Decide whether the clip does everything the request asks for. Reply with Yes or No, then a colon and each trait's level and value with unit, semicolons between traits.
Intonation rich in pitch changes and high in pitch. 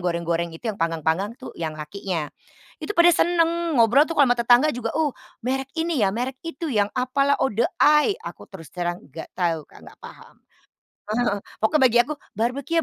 Yes: wide, 8.7 semitones; high, 240 Hz